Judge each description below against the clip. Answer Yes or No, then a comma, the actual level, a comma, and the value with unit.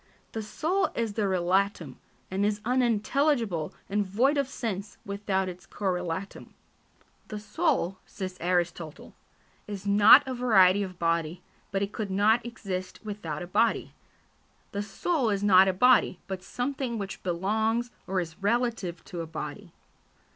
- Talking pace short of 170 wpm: Yes, average, 145 wpm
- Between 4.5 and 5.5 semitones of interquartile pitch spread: No, average, 3.8 semitones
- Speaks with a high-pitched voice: Yes, high, 200 Hz